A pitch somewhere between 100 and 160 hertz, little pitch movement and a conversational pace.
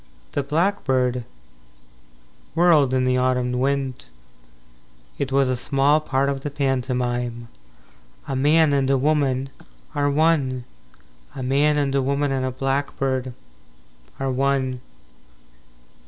No: low, 135 Hz; narrow, 1.8 semitones; slow, 125 wpm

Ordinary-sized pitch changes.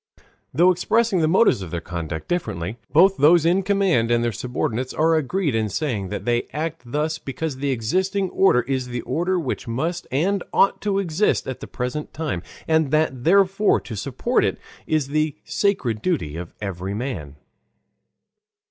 No: wide, 7.0 semitones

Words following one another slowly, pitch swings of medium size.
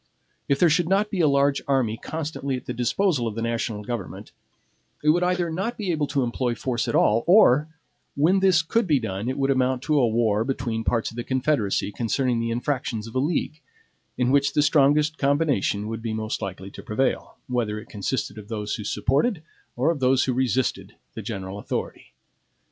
No: average, 200 wpm; average, 5.0 semitones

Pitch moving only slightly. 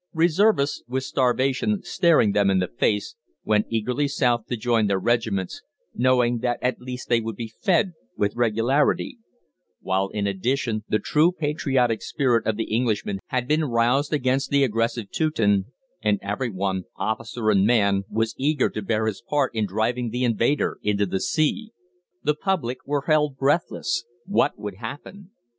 No: average, 4.7 semitones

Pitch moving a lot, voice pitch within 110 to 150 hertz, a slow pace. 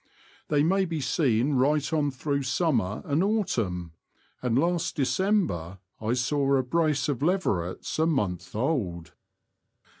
Yes: wide, 6.7 semitones; medium, 140 Hz; slow, 130 wpm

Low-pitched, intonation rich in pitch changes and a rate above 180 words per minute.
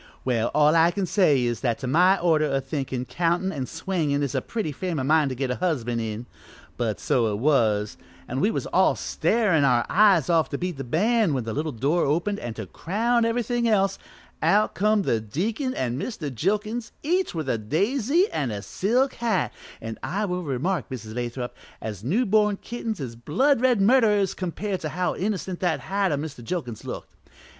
No: medium, 165 Hz; wide, 8.1 semitones; average, 200 wpm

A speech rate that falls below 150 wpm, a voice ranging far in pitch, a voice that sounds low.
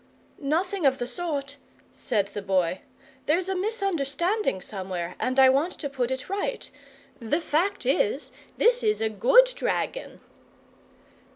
No: slow, 135 wpm; wide, 8.7 semitones; very high, 290 Hz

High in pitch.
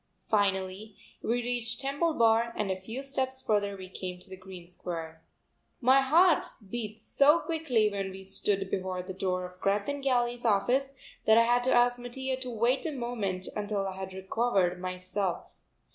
Yes: high, 215 Hz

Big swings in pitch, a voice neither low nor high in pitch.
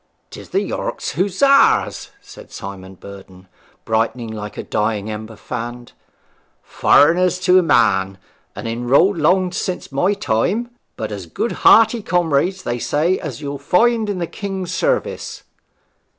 Yes: wide, 9.0 semitones; medium, 145 Hz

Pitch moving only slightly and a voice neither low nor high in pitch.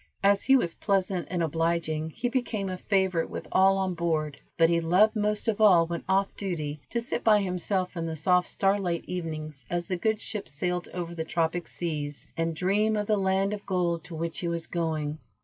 No: average, 3.1 semitones; medium, 180 Hz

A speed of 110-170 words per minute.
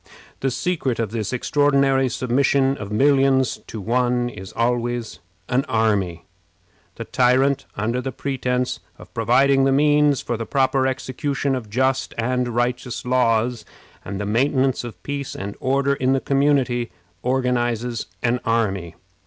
Yes: average, 140 wpm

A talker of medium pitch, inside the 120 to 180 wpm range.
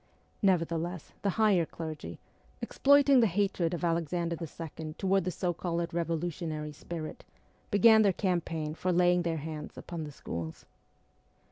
Yes: medium, 170 Hz; average, 140 wpm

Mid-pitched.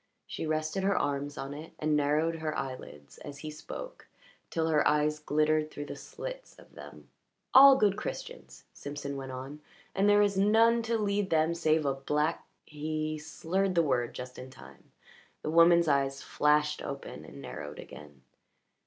Yes: medium, 155 Hz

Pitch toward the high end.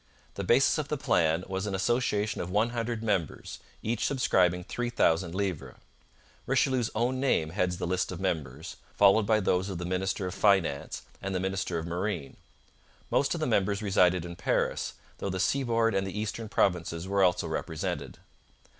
No: very low, 95 Hz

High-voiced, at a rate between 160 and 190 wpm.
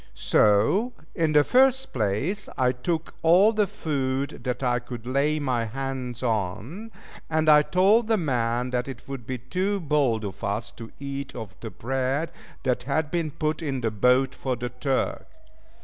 No: low, 135 Hz; average, 170 wpm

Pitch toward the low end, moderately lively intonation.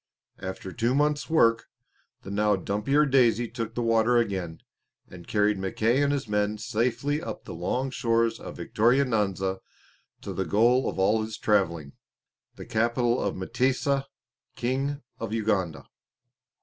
Yes: low, 115 Hz; average, 3.8 semitones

